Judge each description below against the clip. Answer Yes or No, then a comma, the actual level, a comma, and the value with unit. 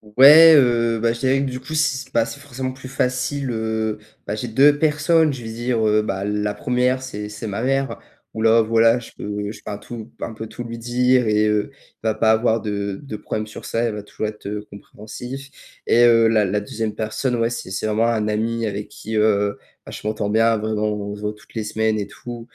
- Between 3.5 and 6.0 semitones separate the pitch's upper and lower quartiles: No, average, 2.8 semitones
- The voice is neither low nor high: No, low, 115 Hz